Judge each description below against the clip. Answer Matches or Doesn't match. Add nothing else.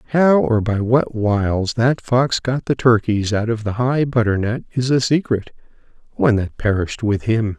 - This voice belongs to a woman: Doesn't match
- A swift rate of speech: Doesn't match